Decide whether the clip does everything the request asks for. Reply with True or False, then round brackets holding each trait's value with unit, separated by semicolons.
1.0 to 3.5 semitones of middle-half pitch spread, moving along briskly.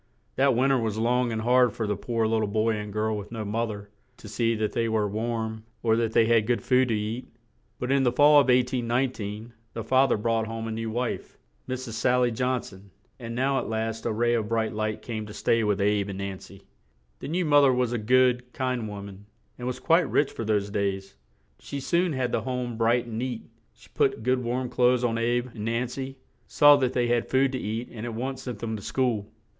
True (2.6 semitones; 240 wpm)